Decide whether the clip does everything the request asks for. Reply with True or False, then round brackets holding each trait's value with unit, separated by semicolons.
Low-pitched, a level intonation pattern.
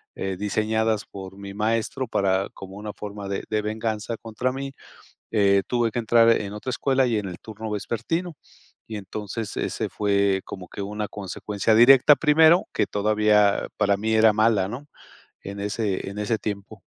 True (105 Hz; 2.3 semitones)